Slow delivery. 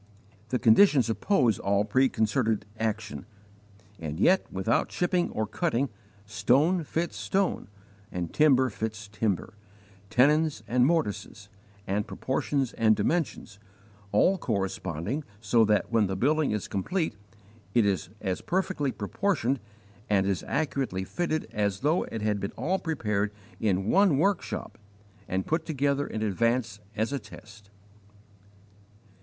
Yes: slow, 125 wpm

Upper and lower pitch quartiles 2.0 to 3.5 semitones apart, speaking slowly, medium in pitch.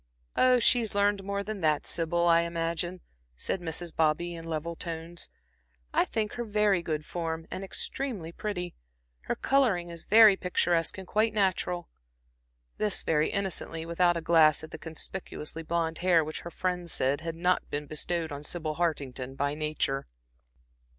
No: average, 3.0 semitones; average, 160 wpm; medium, 170 Hz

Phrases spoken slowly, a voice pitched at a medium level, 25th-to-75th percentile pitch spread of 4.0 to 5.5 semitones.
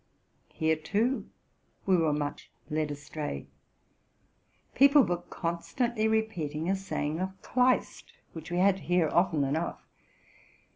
Yes: slow, 130 wpm; medium, 175 Hz; average, 4.6 semitones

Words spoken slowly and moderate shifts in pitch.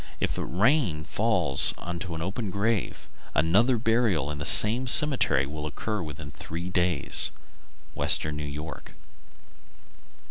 No: slow, 120 wpm; wide, 6.7 semitones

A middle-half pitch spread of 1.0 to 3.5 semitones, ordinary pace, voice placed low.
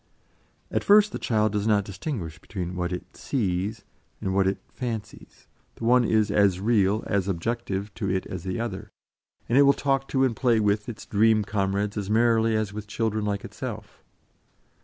Yes: average, 2.8 semitones; average, 180 wpm; low, 105 Hz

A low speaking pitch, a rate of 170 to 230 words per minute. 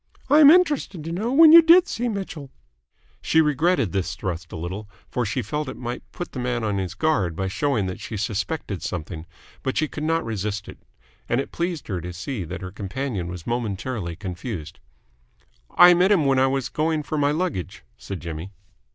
Yes: low, 125 Hz; average, 200 wpm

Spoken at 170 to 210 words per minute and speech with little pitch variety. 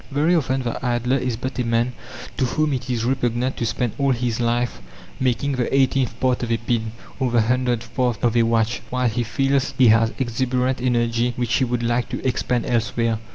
Yes: fast, 205 wpm; narrow, 1.8 semitones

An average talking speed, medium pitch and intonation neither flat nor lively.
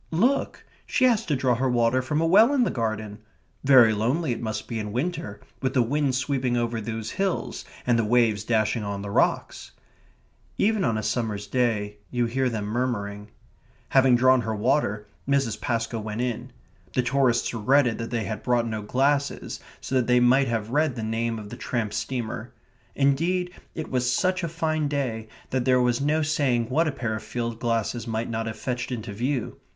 No: average, 195 wpm; low, 120 Hz; average, 3.6 semitones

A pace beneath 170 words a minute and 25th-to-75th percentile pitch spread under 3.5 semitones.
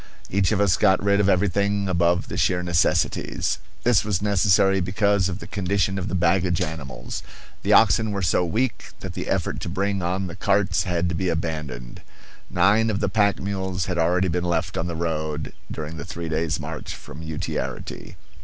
No: average, 190 wpm; average, 3.1 semitones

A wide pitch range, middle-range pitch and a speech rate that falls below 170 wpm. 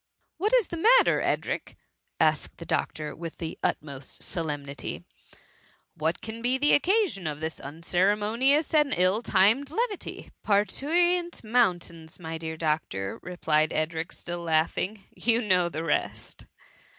Yes: wide, 8.1 semitones; medium, 180 Hz; average, 145 wpm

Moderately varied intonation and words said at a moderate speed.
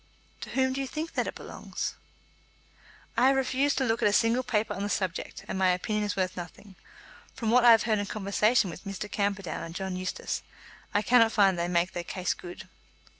No: average, 4.0 semitones; fast, 220 wpm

